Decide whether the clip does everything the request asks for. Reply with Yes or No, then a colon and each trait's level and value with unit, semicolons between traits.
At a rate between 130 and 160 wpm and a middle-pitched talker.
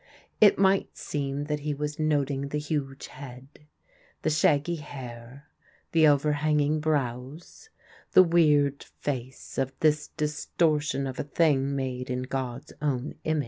Yes: slow, 135 wpm; medium, 145 Hz